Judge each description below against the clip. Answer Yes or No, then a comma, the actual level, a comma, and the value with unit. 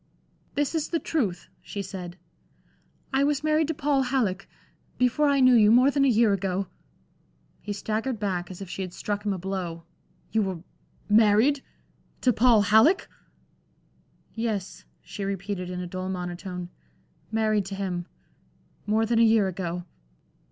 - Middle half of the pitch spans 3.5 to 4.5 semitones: No, average, 5.1 semitones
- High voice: Yes, high, 205 Hz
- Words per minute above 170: No, average, 155 wpm